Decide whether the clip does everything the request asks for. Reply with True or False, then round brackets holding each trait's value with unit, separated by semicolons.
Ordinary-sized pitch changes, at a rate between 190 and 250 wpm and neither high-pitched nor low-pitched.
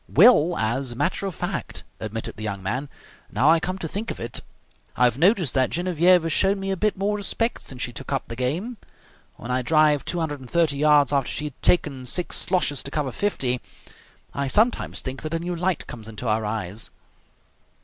False (6.1 semitones; 200 wpm; 150 Hz)